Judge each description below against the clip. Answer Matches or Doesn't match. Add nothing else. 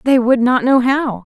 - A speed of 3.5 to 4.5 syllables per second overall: Matches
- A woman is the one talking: Matches